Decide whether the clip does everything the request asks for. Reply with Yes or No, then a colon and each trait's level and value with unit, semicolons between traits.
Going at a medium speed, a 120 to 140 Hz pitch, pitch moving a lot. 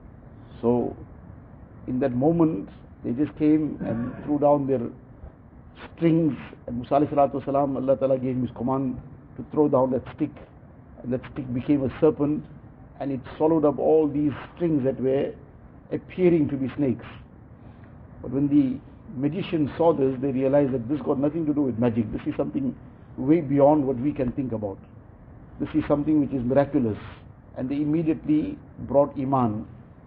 No: average, 160 wpm; low, 135 Hz; average, 3.0 semitones